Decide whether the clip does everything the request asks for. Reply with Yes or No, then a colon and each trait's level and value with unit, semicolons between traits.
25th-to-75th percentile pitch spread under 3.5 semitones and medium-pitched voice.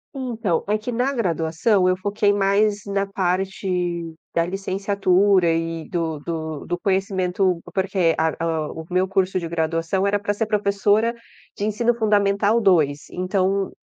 No: average, 2.8 semitones; high, 195 Hz